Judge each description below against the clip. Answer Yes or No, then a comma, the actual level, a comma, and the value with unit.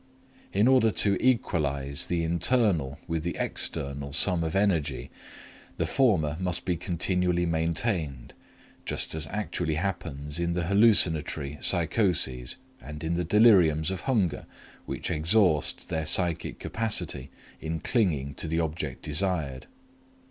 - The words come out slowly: Yes, slow, 125 wpm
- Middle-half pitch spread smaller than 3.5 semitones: No, average, 4.1 semitones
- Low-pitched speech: Yes, very low, 85 Hz